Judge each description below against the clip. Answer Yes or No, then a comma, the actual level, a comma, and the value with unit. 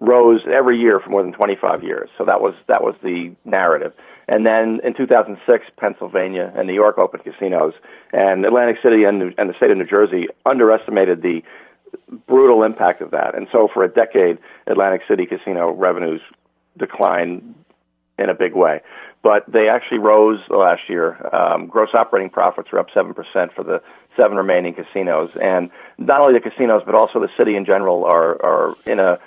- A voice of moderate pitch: No, low, 110 Hz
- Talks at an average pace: Yes, average, 185 wpm